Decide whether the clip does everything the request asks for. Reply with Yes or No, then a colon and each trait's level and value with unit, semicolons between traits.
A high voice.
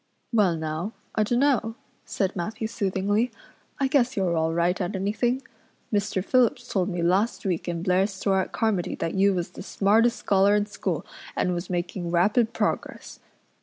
Yes: high, 195 Hz